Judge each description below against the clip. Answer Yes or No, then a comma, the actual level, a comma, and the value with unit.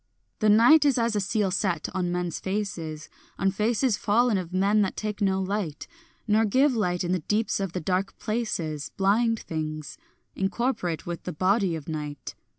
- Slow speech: No, average, 175 wpm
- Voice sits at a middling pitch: No, high, 195 Hz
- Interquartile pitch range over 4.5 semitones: No, average, 3.6 semitones